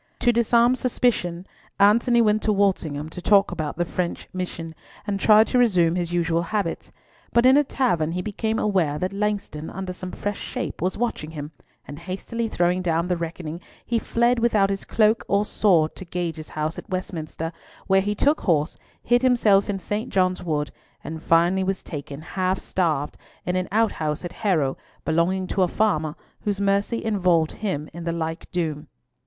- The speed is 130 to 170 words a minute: No, average, 180 wpm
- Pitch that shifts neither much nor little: Yes, average, 4.2 semitones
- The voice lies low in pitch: No, medium, 185 Hz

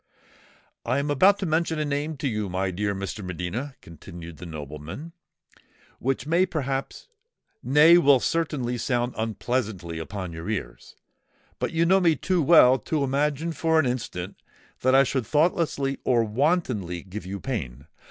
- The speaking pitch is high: No, low, 130 Hz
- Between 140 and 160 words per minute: Yes, average, 155 wpm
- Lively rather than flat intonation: Yes, wide, 8.1 semitones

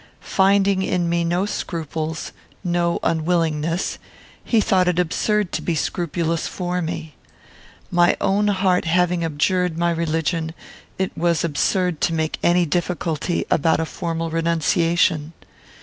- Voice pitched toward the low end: No, medium, 170 Hz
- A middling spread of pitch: No, narrow, 1.8 semitones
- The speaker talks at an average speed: No, slow, 130 wpm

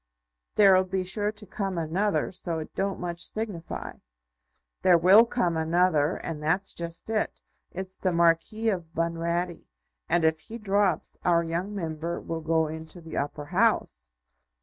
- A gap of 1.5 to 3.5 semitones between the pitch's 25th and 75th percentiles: Yes, average, 2.9 semitones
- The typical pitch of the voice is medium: Yes, medium, 175 Hz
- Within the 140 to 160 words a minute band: Yes, average, 150 wpm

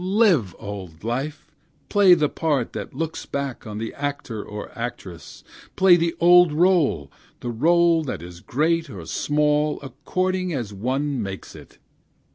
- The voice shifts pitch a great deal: Yes, wide, 7.1 semitones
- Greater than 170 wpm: No, average, 145 wpm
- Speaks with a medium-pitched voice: Yes, medium, 145 Hz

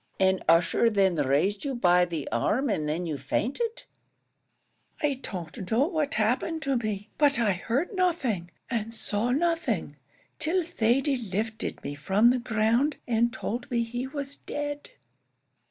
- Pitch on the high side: Yes, high, 230 Hz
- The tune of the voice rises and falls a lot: Yes, wide, 6.5 semitones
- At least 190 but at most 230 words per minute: No, average, 150 wpm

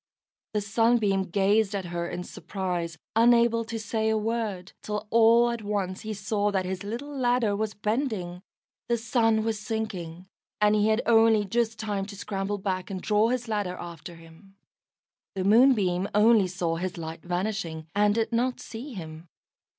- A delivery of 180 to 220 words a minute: No, average, 165 wpm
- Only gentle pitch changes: No, average, 3.3 semitones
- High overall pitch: Yes, high, 210 Hz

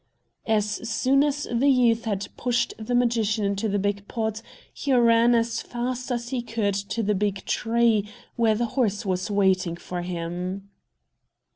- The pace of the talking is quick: No, average, 160 wpm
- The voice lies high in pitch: Yes, high, 220 Hz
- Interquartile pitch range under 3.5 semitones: Yes, average, 3.1 semitones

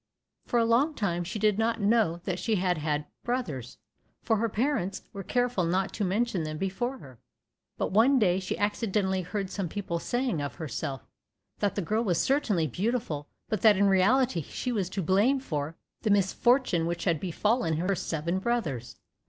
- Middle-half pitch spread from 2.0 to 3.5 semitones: No, average, 5.1 semitones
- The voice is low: No, high, 195 Hz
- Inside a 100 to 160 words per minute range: No, average, 180 wpm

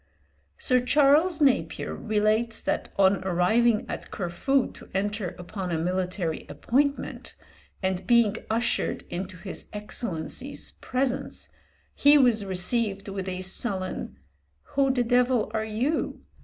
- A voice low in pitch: No, high, 215 Hz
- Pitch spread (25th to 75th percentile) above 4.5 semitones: Yes, average, 4.9 semitones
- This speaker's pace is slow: Yes, slow, 120 wpm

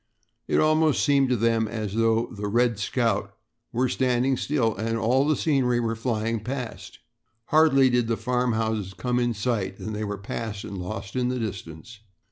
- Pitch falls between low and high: No, low, 115 Hz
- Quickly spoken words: No, average, 175 wpm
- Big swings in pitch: No, average, 2.8 semitones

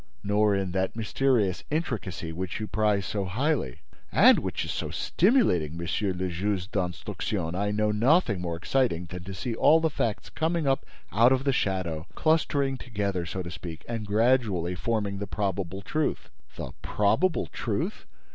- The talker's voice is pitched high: No, low, 105 Hz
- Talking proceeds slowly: No, average, 165 wpm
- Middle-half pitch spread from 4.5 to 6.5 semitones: Yes, wide, 5.6 semitones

